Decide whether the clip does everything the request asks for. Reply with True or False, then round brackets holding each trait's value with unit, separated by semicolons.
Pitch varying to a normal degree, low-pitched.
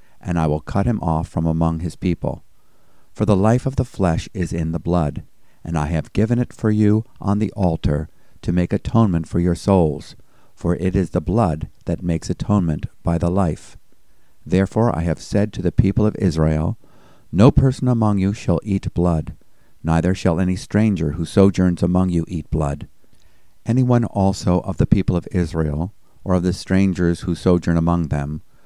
True (3.6 semitones; 90 Hz)